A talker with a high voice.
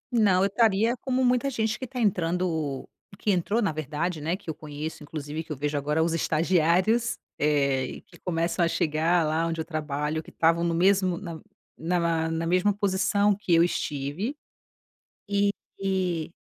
No: medium, 170 Hz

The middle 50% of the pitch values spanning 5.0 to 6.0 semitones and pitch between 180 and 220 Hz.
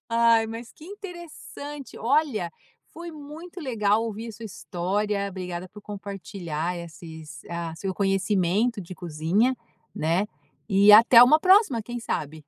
Yes: wide, 5.6 semitones; high, 210 Hz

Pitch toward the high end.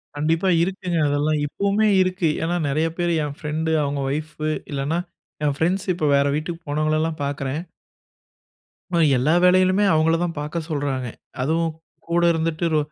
No: medium, 160 Hz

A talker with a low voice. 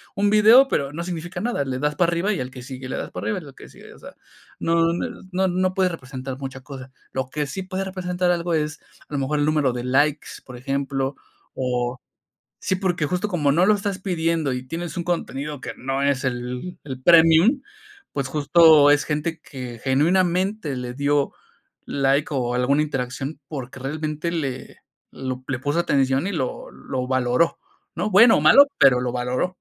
No: medium, 145 Hz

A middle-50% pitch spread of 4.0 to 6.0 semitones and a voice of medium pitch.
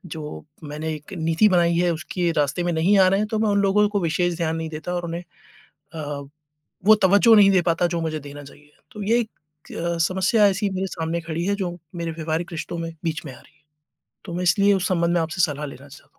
No: average, 3.3 semitones; medium, 170 Hz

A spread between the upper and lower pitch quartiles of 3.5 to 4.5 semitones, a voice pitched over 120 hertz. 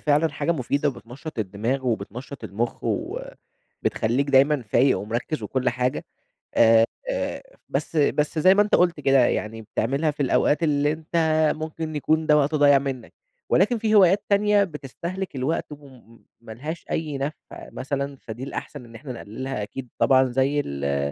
Yes: average, 4.2 semitones; medium, 140 Hz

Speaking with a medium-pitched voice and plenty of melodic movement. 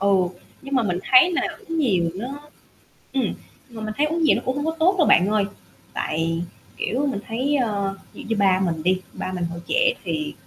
No: high, 225 Hz; wide, 7.6 semitones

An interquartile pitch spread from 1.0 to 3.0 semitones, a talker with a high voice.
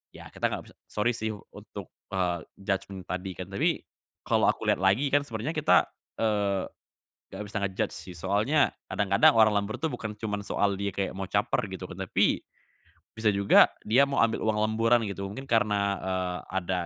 No: narrow, 2.5 semitones; low, 100 Hz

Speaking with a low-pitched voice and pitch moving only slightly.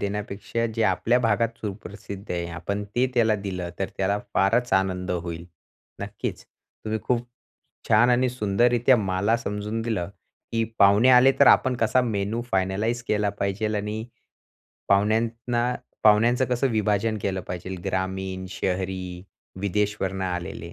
No: low, 105 Hz; average, 3.3 semitones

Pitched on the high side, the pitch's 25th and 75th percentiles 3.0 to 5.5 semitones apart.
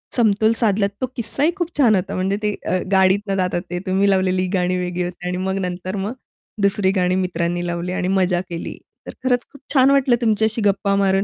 Yes: high, 195 Hz; average, 3.3 semitones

